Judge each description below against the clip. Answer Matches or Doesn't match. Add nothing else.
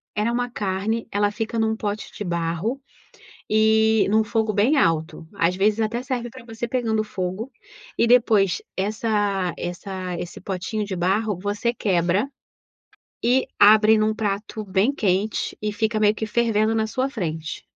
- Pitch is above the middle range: Matches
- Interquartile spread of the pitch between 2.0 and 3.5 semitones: Matches